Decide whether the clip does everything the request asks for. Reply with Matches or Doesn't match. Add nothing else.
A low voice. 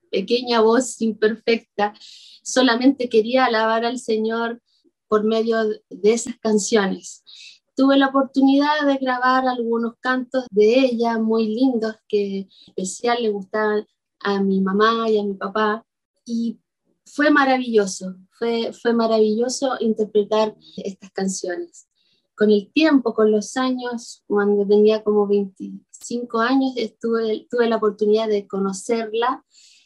Doesn't match